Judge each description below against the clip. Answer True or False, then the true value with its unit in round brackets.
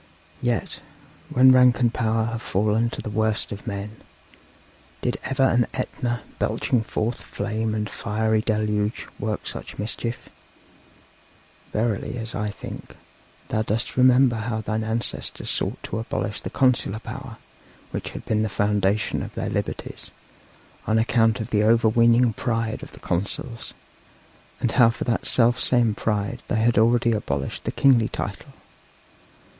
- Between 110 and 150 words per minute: True (145 wpm)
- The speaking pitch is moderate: False (110 Hz)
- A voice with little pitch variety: True (1.9 semitones)